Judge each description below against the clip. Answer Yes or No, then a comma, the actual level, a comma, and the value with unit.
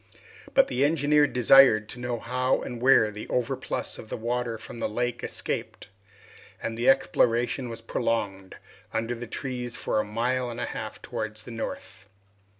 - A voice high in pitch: No, low, 120 Hz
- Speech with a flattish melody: Yes, narrow, 2.1 semitones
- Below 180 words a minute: Yes, average, 165 wpm